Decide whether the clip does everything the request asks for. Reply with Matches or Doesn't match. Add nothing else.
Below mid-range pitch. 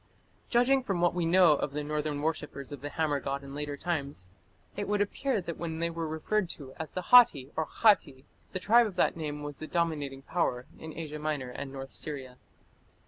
Doesn't match